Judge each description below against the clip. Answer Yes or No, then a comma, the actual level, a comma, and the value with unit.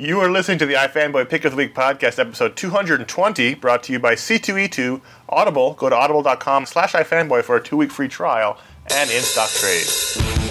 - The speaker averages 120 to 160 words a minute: No, average, 190 wpm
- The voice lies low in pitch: No, medium, 155 Hz